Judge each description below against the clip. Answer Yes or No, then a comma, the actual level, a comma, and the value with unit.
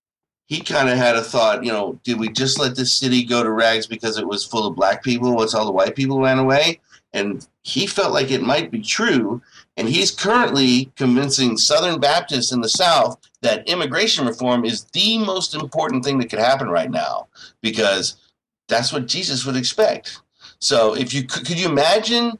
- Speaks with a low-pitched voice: Yes, low, 130 Hz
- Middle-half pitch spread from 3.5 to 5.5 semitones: Yes, average, 4.1 semitones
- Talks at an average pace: Yes, average, 195 wpm